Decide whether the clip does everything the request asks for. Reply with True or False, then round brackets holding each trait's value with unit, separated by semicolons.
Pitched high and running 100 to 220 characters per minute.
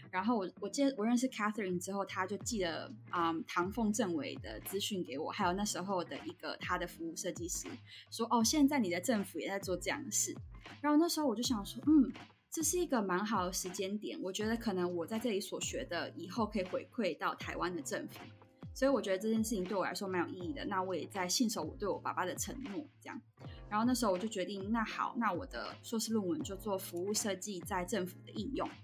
False (200 Hz; 360 characters per minute)